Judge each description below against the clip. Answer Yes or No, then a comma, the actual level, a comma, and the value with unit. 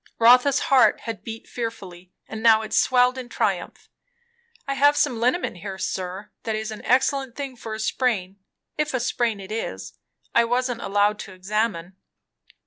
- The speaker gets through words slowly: No, average, 165 wpm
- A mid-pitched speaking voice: No, high, 225 Hz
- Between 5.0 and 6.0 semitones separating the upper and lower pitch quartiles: No, average, 3.6 semitones